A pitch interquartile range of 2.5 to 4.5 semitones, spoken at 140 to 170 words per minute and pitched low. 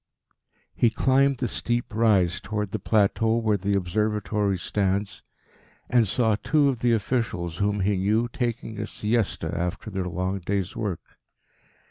Yes: average, 3.1 semitones; average, 145 wpm; low, 105 Hz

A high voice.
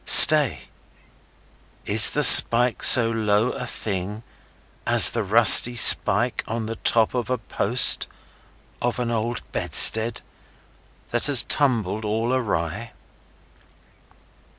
No: low, 115 Hz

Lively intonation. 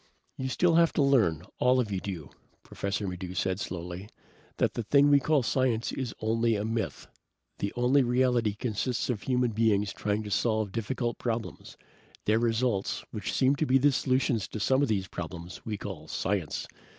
No: average, 4.2 semitones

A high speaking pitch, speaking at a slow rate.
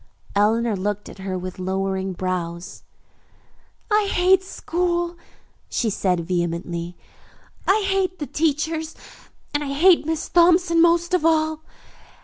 Yes: very high, 295 Hz; slow, 125 wpm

